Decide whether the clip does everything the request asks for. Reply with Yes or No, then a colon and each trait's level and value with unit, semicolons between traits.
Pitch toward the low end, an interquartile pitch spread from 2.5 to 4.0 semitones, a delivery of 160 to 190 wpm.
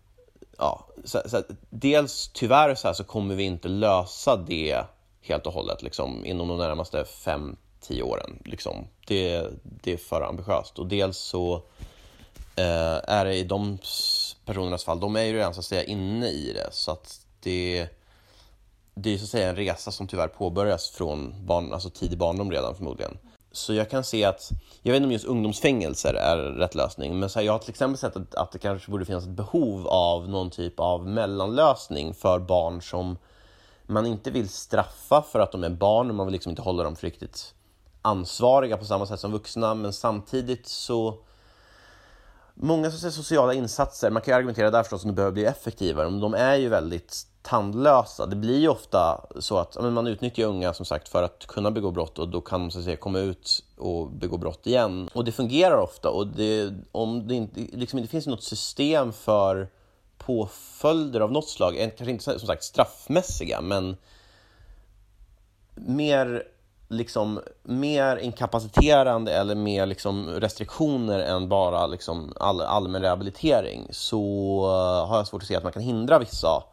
Yes: low, 100 Hz; average, 3.7 semitones; average, 180 wpm